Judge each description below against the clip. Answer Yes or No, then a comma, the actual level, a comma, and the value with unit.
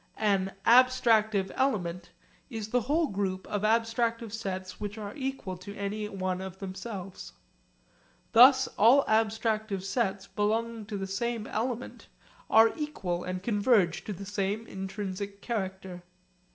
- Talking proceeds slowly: Yes, slow, 130 wpm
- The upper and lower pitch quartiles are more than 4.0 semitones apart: No, average, 3.1 semitones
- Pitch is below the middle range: No, high, 210 Hz